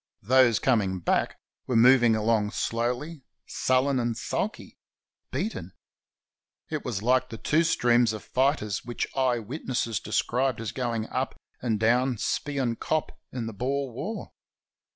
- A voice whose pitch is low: Yes, low, 120 Hz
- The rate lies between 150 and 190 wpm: No, average, 140 wpm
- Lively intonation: No, average, 2.7 semitones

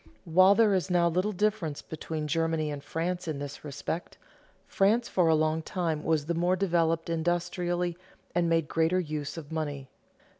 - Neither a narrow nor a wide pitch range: No, narrow, 2.3 semitones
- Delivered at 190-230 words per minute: No, average, 165 wpm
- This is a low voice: No, medium, 165 Hz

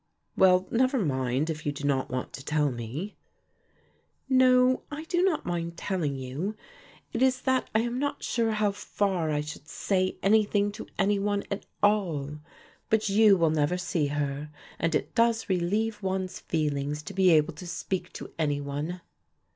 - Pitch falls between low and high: Yes, medium, 180 Hz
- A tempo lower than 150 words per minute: No, average, 170 wpm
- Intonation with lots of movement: Yes, wide, 6.1 semitones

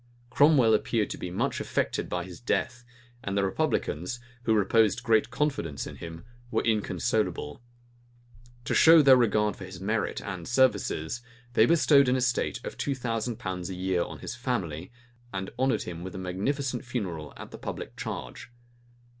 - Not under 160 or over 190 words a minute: Yes, average, 165 wpm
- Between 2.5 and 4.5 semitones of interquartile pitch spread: No, average, 5.2 semitones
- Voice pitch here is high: No, low, 110 Hz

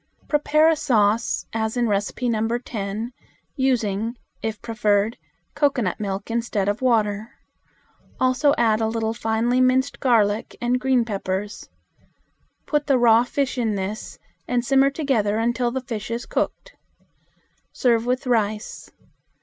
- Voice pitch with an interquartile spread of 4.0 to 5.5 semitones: No, average, 3.0 semitones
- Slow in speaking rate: Yes, slow, 130 wpm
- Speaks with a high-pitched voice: Yes, high, 230 Hz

